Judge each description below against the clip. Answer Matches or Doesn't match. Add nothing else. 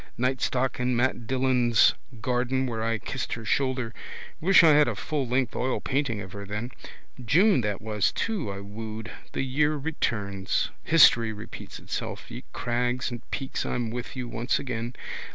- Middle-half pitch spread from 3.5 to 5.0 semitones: Doesn't match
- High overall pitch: Doesn't match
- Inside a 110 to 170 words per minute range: Matches